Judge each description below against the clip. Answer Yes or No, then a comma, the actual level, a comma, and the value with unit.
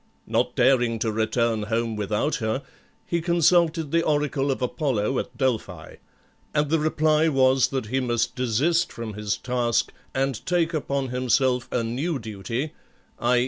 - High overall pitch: No, low, 130 Hz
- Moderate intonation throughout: Yes, average, 4.5 semitones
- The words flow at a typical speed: Yes, average, 150 wpm